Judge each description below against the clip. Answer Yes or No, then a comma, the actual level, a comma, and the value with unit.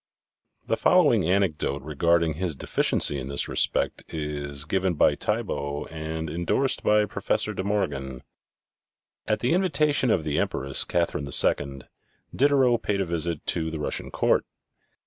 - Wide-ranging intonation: Yes, wide, 5.7 semitones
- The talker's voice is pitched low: Yes, very low, 80 Hz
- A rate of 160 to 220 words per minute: No, average, 140 wpm